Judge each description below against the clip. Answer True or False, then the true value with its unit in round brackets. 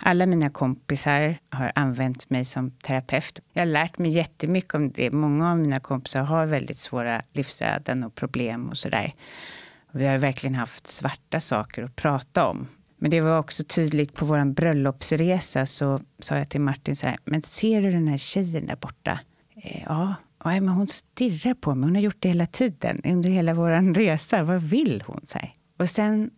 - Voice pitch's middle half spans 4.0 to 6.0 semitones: True (4.5 semitones)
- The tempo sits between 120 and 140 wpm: False (185 wpm)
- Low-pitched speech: False (155 Hz)